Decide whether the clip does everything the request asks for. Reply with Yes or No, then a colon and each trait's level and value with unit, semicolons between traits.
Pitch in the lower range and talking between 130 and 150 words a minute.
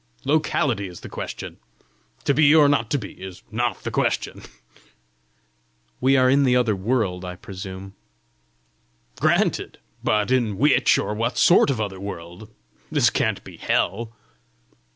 Yes: low, 110 Hz; average, 145 wpm